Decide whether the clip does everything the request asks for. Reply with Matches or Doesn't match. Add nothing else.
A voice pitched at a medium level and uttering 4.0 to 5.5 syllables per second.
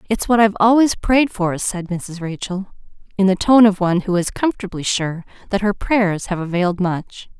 Doesn't match